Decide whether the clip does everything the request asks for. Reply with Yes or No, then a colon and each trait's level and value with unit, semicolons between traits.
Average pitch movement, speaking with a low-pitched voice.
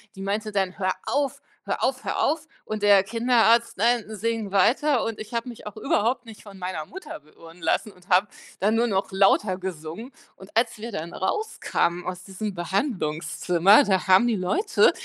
No: average, 3.9 semitones; high, 205 Hz